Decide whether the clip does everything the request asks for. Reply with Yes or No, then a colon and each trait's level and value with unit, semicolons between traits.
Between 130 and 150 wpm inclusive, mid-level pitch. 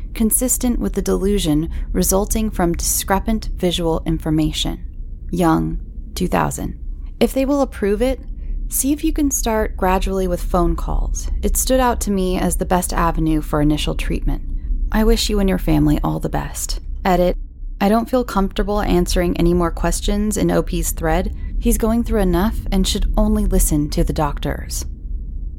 No: average, 160 wpm; medium, 180 Hz